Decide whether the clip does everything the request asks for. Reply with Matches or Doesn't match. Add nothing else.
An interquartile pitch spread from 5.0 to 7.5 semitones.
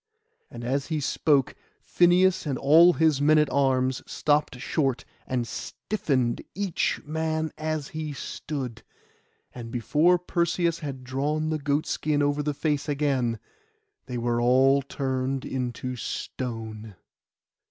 Doesn't match